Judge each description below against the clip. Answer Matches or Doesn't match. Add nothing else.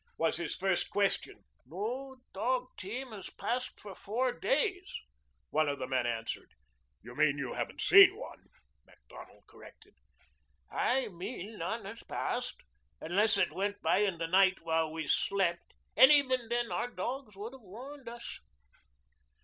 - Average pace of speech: Matches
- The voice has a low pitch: Doesn't match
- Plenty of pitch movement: Matches